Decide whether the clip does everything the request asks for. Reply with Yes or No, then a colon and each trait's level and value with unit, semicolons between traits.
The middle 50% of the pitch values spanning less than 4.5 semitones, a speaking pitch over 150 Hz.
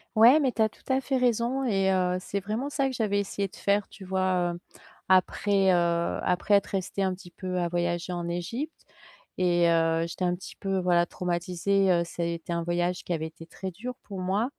Yes: average, 2.7 semitones; medium, 185 Hz